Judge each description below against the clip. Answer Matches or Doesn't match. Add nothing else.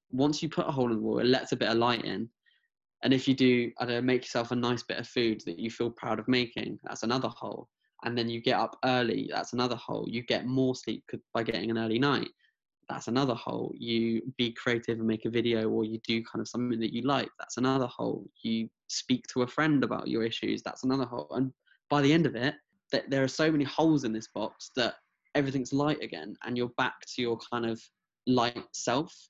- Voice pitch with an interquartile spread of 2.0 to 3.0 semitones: Matches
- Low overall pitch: Matches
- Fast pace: Matches